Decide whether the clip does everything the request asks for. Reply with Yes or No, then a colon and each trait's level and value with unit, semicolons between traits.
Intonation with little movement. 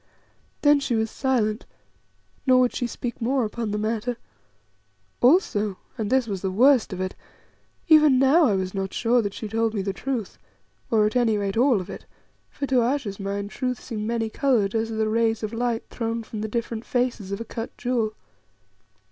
No: average, 3.0 semitones